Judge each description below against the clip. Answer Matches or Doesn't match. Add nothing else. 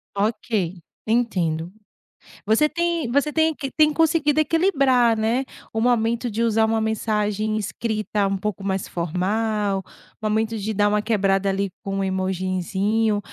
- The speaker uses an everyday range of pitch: Matches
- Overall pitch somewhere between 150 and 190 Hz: Doesn't match